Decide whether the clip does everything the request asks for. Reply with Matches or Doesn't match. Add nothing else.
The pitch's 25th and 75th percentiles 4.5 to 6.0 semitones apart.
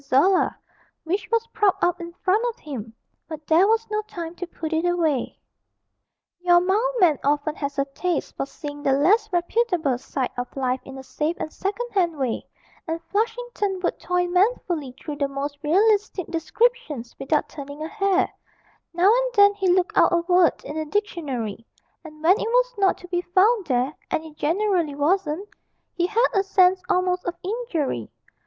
Matches